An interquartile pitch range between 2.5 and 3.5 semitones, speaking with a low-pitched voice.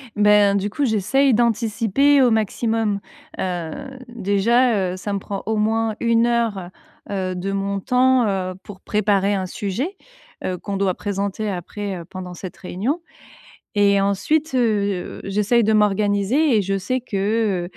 No: average, 2.9 semitones; high, 205 Hz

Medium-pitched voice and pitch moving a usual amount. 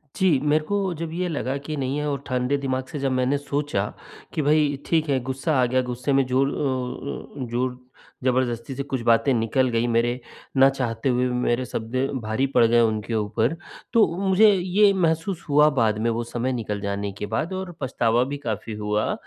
No: low, 130 Hz; average, 3.8 semitones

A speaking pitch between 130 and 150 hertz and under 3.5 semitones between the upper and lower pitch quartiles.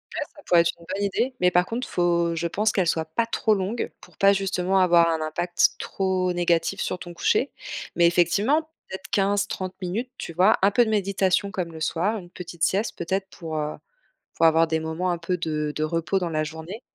No: medium, 180 Hz; average, 2.9 semitones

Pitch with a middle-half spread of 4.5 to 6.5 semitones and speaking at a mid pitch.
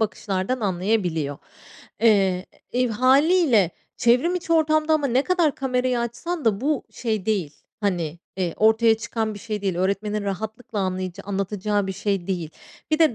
No: average, 4.8 semitones; high, 215 Hz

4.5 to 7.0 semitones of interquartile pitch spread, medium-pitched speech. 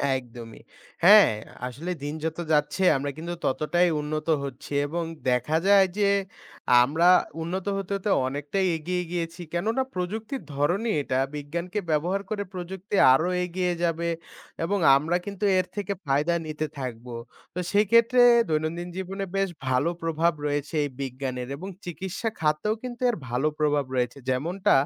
Yes: average, 4.8 semitones; medium, 170 Hz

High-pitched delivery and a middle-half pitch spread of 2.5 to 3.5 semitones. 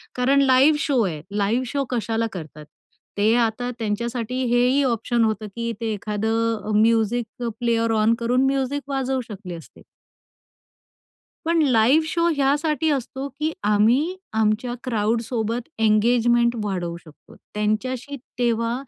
Yes: high, 235 Hz; average, 3.1 semitones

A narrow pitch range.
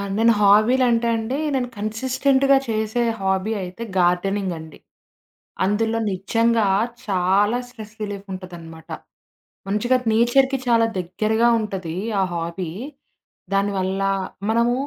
No: average, 3.7 semitones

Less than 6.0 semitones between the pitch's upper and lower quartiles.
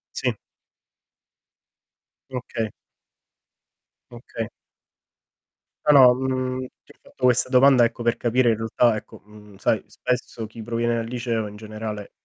Yes: narrow, 2.4 semitones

